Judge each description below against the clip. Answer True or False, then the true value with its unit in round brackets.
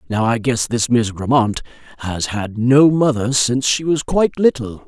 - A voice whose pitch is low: True (120 Hz)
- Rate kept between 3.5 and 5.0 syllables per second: True (4.7 syllables/s)